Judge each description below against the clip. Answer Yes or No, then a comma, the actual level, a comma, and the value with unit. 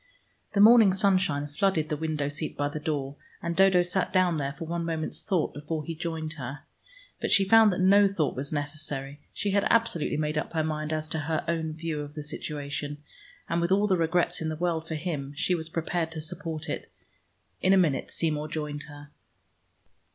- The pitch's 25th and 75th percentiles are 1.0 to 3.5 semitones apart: Yes, average, 3.1 semitones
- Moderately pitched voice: Yes, medium, 160 Hz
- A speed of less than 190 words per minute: No, fast, 205 wpm